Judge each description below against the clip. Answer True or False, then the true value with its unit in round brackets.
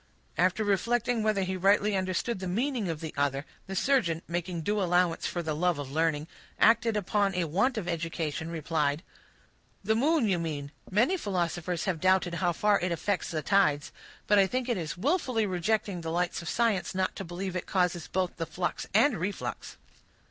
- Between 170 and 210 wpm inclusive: True (185 wpm)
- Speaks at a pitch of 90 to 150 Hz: False (185 Hz)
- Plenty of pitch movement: False (3.9 semitones)